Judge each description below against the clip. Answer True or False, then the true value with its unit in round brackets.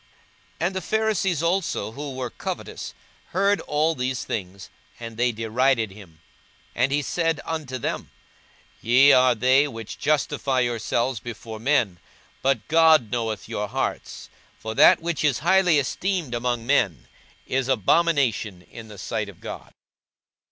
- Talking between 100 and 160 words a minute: True (145 wpm)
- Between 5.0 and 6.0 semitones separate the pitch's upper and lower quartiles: True (5.5 semitones)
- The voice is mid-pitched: False (130 Hz)